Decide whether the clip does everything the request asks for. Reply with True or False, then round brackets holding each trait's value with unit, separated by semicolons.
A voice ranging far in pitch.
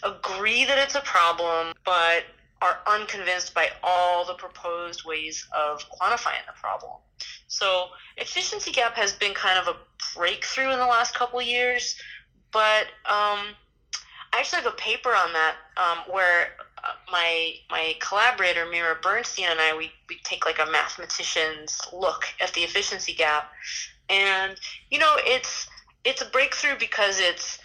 True (6.4 semitones)